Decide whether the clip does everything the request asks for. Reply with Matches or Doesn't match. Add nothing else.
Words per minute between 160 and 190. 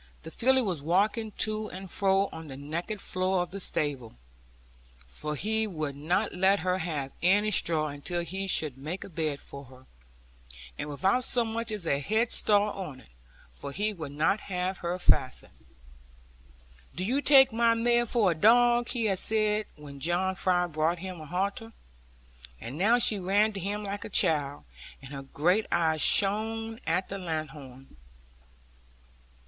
Matches